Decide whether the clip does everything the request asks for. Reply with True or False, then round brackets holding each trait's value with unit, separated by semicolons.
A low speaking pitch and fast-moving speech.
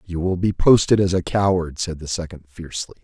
True (85 Hz; 220 wpm)